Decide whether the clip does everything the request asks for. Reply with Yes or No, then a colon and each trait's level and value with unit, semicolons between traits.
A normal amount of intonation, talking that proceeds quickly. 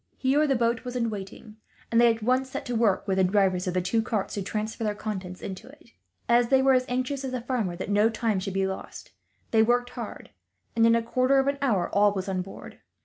Yes: average, 4.2 semitones; fast, 250 wpm